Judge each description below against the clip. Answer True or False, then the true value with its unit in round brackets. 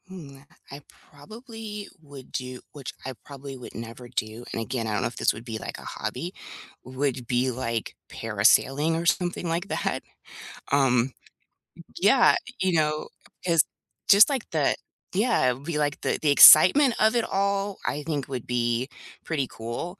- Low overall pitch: False (145 Hz)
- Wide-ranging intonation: True (6.1 semitones)